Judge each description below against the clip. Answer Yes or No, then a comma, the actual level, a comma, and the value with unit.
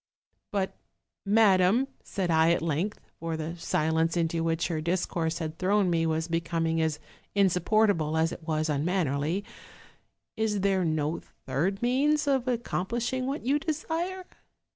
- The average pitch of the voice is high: No, medium, 175 Hz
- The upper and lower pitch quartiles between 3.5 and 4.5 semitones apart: No, average, 5.0 semitones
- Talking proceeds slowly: No, average, 145 wpm